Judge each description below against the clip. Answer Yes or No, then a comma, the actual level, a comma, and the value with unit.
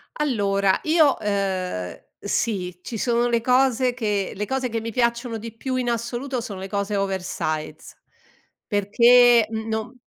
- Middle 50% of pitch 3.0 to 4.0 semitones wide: Yes, average, 3.5 semitones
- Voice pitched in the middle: No, high, 225 Hz